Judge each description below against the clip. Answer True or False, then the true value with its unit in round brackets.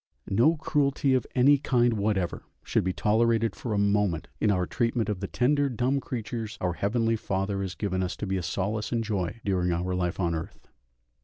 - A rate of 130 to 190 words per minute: False (200 wpm)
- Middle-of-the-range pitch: False (105 Hz)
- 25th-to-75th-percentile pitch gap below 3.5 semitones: False (4.2 semitones)